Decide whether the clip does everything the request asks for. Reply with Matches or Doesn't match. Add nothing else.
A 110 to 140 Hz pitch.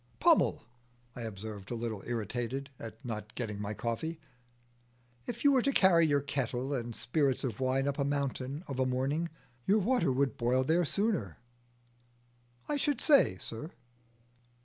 Matches